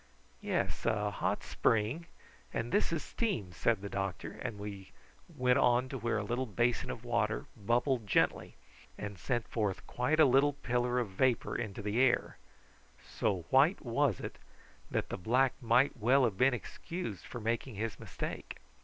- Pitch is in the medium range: No, low, 120 Hz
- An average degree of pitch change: Yes, average, 3.8 semitones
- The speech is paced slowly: No, average, 165 wpm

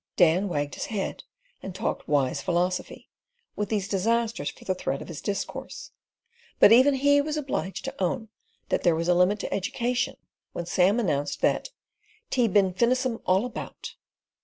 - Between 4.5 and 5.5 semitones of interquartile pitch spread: Yes, average, 5.0 semitones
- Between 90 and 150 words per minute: No, average, 165 wpm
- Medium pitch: No, high, 200 Hz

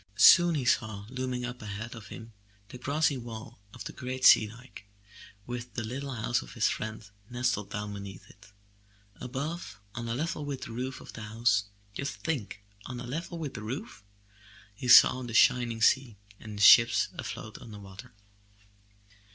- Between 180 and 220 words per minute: Yes, average, 185 wpm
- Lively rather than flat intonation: No, average, 3.6 semitones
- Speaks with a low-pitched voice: Yes, low, 120 Hz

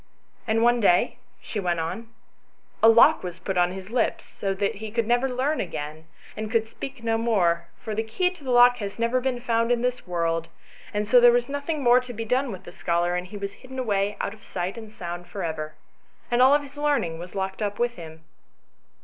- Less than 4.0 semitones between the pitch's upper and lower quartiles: No, average, 5.1 semitones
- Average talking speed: No, fast, 220 wpm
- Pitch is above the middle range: Yes, high, 220 Hz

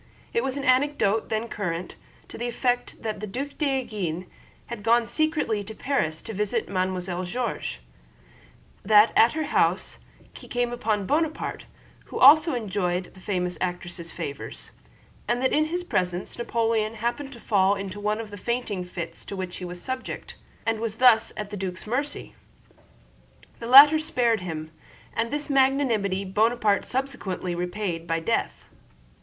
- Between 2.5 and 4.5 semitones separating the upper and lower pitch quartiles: No, average, 5.2 semitones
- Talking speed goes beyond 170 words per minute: No, average, 155 wpm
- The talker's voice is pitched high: Yes, high, 215 Hz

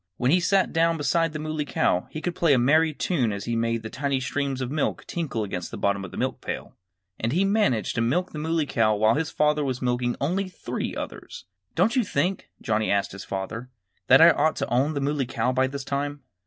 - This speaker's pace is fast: Yes, fast, 235 wpm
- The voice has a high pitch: No, medium, 140 Hz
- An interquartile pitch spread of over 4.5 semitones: Yes, wide, 5.5 semitones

